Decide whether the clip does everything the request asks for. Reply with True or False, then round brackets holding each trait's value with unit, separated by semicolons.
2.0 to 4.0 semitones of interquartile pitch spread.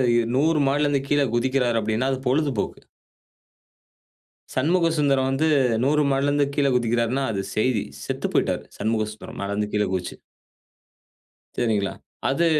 False (4.6 semitones)